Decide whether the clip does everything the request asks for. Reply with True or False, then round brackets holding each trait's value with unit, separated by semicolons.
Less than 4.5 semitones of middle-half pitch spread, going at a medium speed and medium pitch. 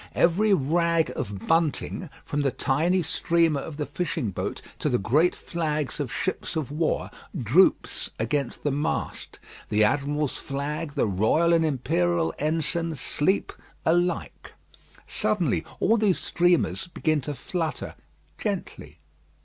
False (3.7 semitones; 130 wpm; 155 Hz)